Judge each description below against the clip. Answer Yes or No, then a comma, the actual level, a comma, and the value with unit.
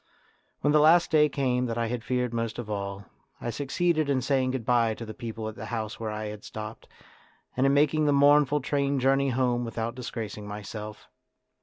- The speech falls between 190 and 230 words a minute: Yes, average, 195 wpm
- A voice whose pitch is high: No, low, 125 Hz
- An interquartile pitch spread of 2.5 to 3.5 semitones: No, average, 4.0 semitones